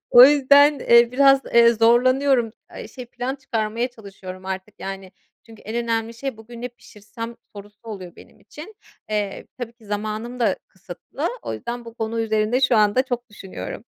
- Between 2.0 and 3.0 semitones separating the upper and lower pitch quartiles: Yes, average, 2.7 semitones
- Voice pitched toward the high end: Yes, high, 230 Hz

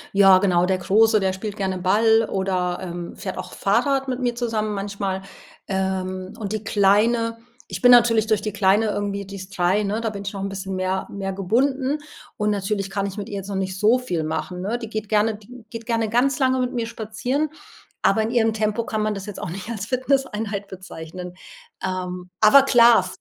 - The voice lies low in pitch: No, high, 205 Hz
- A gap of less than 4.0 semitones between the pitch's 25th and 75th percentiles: Yes, average, 3.1 semitones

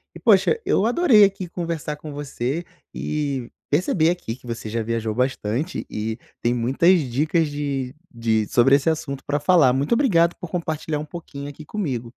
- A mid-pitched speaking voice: Yes, medium, 145 Hz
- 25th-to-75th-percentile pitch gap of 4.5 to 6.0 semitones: Yes, wide, 5.4 semitones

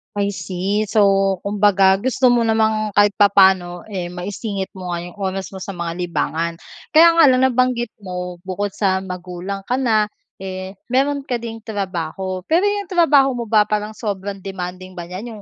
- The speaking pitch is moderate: No, high, 200 Hz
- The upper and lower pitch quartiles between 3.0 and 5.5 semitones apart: Yes, average, 3.4 semitones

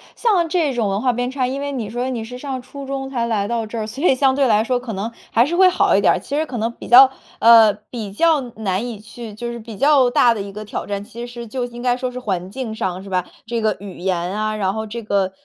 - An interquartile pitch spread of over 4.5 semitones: No, average, 3.5 semitones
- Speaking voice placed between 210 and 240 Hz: Yes, high, 235 Hz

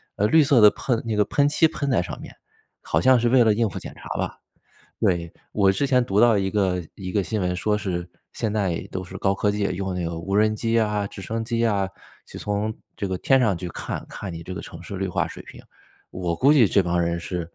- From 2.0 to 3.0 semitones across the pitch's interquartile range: No, average, 3.9 semitones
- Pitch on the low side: Yes, low, 100 Hz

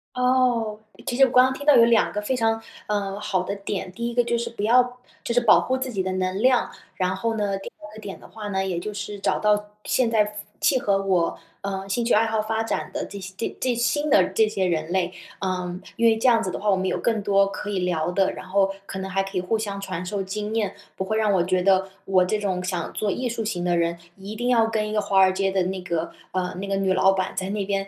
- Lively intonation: No, average, 3.0 semitones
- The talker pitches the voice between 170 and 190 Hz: No, high, 200 Hz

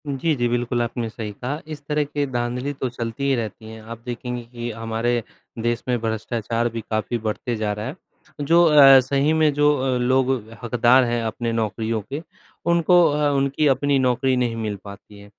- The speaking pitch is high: No, low, 120 Hz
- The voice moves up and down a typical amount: Yes, average, 3.3 semitones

